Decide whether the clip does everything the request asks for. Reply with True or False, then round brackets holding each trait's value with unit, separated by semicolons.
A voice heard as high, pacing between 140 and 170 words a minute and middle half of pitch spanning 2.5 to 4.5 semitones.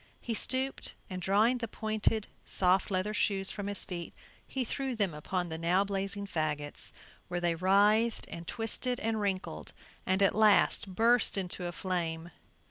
True (195 Hz; 160 wpm; 3.5 semitones)